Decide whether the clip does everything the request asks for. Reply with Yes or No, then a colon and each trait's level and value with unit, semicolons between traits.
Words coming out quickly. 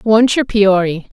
No: average, 150 wpm